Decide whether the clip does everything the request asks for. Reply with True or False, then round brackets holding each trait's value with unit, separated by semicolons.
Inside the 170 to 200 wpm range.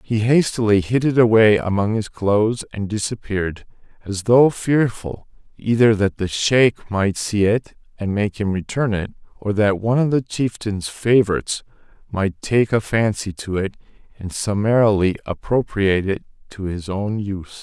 False (155 wpm)